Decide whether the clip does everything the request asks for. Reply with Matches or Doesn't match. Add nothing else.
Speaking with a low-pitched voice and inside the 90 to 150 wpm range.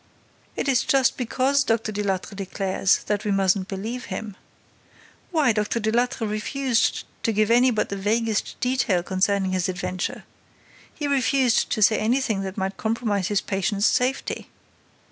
Doesn't match